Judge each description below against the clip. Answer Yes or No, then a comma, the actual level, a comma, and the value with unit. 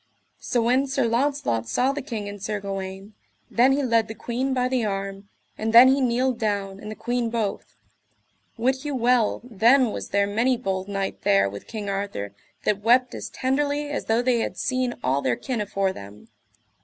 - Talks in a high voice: Yes, high, 230 Hz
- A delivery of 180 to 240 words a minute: Yes, average, 190 wpm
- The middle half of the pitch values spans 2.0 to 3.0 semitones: No, average, 4.4 semitones